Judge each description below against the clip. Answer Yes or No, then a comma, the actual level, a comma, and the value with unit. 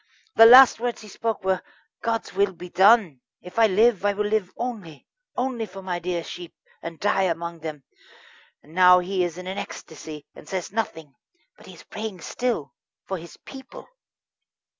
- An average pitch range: Yes, average, 4.5 semitones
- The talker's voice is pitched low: No, high, 190 Hz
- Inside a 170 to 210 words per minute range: Yes, average, 180 wpm